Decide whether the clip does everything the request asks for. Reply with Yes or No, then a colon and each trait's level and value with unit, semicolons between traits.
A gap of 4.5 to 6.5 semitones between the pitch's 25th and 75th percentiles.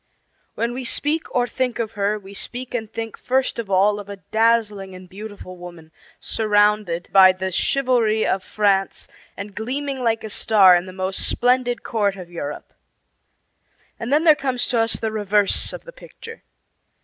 No: average, 4.0 semitones